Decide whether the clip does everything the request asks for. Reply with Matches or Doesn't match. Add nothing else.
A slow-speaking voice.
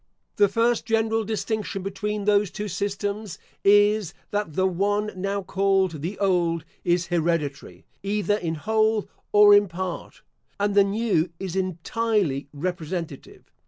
Matches